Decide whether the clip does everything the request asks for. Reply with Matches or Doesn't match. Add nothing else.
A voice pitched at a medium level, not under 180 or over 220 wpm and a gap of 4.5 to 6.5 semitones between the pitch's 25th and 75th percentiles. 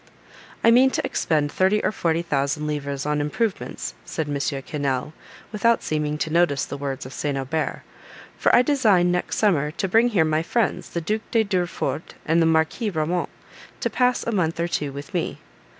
Matches